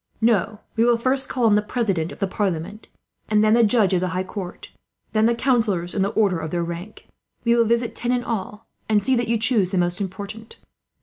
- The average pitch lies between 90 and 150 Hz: No, high, 215 Hz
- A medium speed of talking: No, fast, 230 wpm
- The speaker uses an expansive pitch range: No, average, 3.8 semitones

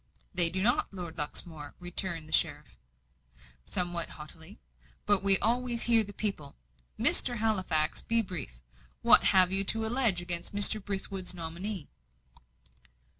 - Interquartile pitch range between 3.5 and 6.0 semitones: Yes, average, 3.9 semitones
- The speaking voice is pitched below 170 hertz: No, high, 190 Hz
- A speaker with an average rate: No, slow, 130 wpm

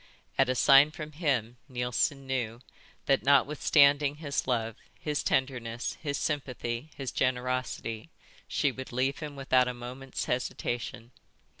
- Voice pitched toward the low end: Yes, low, 130 Hz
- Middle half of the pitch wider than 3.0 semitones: No, narrow, 2.5 semitones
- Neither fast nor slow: No, slow, 130 wpm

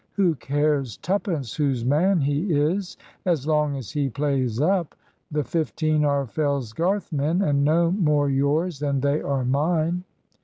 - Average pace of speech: Yes, average, 150 wpm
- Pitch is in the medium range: Yes, medium, 150 Hz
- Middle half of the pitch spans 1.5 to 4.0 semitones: Yes, average, 3.1 semitones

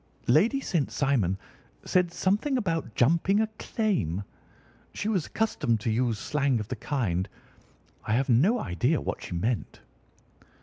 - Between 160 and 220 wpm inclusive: No, average, 140 wpm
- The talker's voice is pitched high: No, medium, 140 Hz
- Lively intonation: Yes, wide, 9.0 semitones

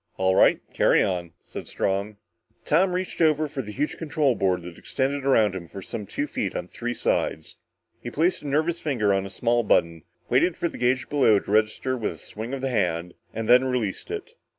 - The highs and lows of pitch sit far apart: Yes, wide, 6.7 semitones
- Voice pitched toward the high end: No, low, 120 Hz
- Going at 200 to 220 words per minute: Yes, fast, 205 wpm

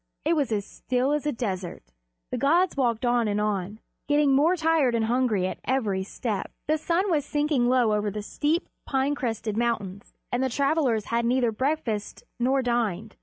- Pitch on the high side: Yes, high, 245 Hz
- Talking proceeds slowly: No, average, 180 wpm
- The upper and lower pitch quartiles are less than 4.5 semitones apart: No, average, 5.2 semitones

